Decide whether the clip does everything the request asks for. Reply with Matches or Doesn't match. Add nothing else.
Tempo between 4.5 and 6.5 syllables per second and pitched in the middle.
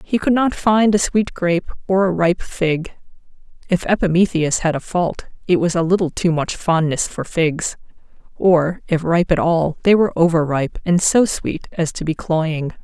Doesn't match